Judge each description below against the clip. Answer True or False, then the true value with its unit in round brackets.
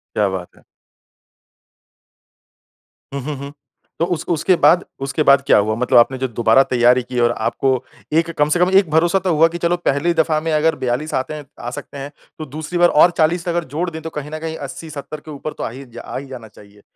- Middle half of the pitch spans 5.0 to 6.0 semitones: False (4.3 semitones)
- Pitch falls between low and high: True (150 Hz)